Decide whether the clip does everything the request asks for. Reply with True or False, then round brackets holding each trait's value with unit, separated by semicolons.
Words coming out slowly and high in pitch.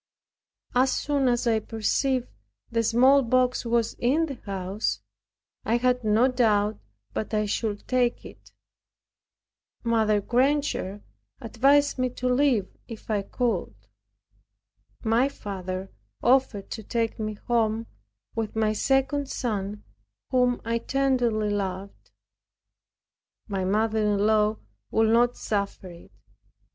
True (115 wpm; 230 Hz)